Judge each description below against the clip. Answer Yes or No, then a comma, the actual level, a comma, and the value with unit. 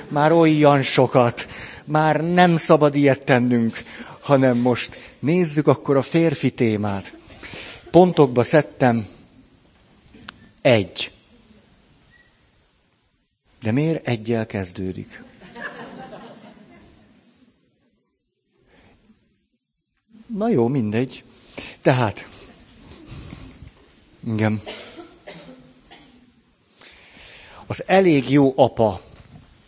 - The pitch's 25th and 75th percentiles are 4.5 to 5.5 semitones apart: Yes, average, 5.0 semitones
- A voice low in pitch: Yes, low, 130 Hz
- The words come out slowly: Yes, slow, 65 wpm